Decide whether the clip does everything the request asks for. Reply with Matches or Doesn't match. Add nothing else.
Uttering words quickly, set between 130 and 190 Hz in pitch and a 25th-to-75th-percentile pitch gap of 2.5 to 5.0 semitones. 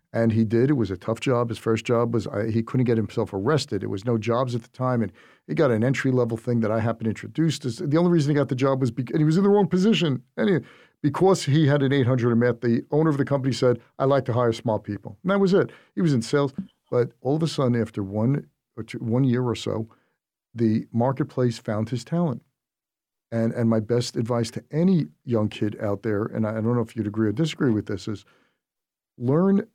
Doesn't match